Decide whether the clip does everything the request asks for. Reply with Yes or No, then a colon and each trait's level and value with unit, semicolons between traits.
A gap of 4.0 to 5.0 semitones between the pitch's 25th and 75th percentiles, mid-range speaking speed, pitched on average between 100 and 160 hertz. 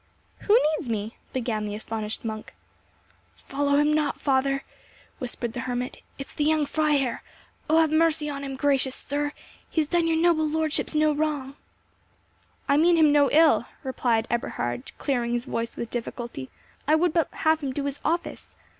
No: average, 4.3 semitones; average, 170 wpm; very high, 285 Hz